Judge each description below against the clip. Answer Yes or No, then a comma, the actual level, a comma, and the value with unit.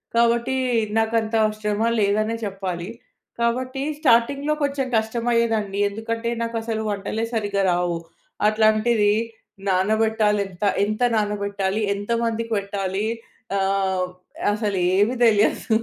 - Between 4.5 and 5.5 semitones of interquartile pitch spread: No, narrow, 2.4 semitones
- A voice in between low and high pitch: No, high, 215 Hz